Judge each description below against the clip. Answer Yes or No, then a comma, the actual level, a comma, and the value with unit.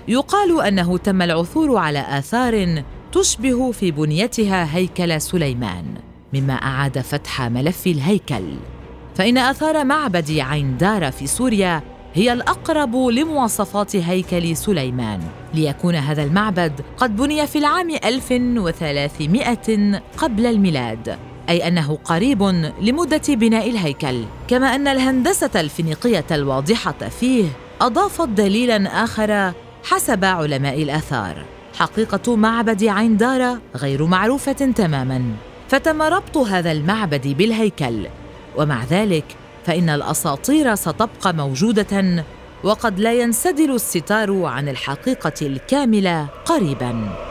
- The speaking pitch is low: No, medium, 185 Hz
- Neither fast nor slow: Yes, average, 105 wpm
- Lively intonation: Yes, wide, 8.3 semitones